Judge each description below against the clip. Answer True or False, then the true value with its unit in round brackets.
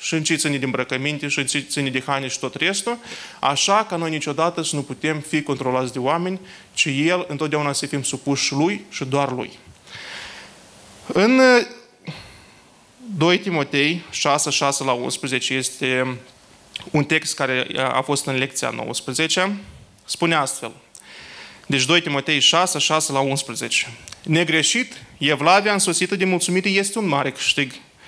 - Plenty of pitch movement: False (4.2 semitones)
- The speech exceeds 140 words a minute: True (150 wpm)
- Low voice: False (145 Hz)